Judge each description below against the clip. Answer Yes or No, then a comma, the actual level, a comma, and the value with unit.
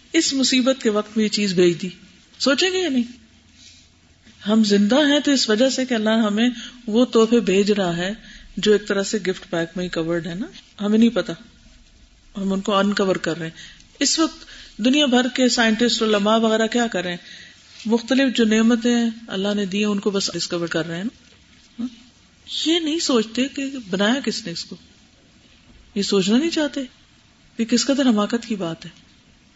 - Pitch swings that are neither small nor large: Yes, average, 4.1 semitones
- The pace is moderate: No, fast, 195 wpm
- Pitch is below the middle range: No, high, 220 Hz